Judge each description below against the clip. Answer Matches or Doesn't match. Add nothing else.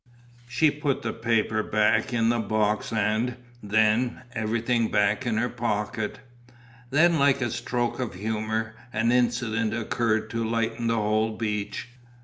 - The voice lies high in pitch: Doesn't match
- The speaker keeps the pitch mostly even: Matches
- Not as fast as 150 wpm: Matches